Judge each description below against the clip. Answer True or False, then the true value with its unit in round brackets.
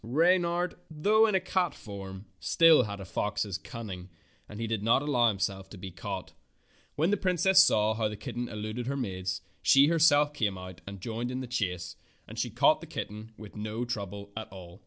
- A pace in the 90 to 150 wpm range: False (205 wpm)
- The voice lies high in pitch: False (110 Hz)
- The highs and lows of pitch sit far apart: True (6.7 semitones)